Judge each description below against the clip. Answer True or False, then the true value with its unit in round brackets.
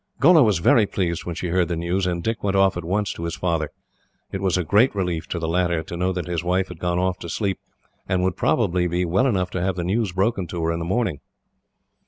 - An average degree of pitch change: False (2.1 semitones)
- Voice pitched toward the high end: False (90 Hz)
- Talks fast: True (260 wpm)